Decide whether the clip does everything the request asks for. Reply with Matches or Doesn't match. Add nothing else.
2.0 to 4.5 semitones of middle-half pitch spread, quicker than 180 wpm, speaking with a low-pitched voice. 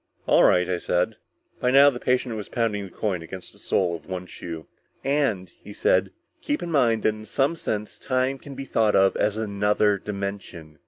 Doesn't match